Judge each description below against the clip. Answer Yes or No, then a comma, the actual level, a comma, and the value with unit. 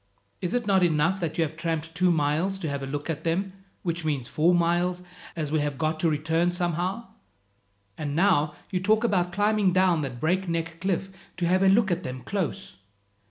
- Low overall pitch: No, medium, 170 Hz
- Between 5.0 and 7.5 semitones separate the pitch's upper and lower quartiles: No, average, 3.2 semitones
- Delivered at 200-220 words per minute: Yes, fast, 205 wpm